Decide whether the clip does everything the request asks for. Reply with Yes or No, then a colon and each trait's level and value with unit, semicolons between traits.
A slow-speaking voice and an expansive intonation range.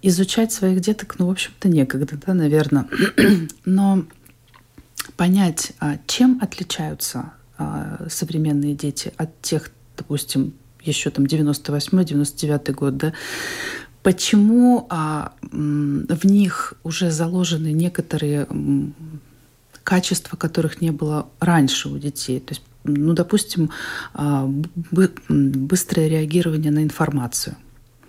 No: slow, 95 wpm; average, 4.1 semitones